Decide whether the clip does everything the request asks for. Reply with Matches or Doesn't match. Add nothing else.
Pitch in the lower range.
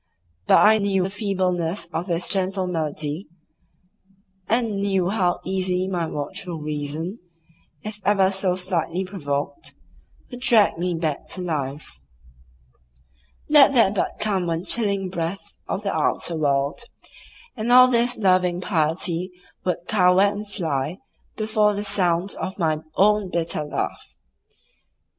Doesn't match